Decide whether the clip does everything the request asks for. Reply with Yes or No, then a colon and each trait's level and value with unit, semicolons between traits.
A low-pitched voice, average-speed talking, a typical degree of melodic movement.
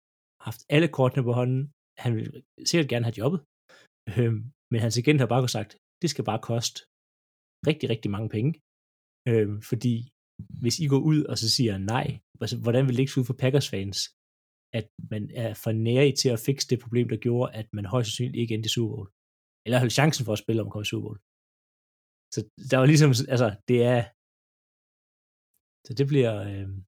Yes: low, 120 Hz; average, 190 wpm; average, 3.4 semitones